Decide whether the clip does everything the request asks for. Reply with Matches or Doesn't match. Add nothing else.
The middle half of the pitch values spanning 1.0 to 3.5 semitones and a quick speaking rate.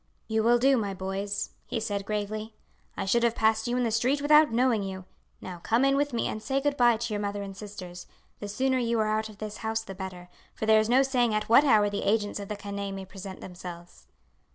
Matches